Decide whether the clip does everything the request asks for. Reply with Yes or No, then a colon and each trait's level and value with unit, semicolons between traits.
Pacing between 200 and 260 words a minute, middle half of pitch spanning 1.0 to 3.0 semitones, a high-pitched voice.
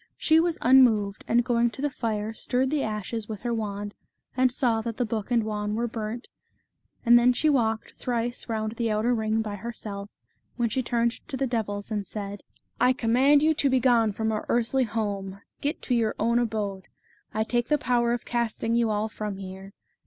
Yes: fast, 205 wpm; narrow, 2.4 semitones; high, 230 Hz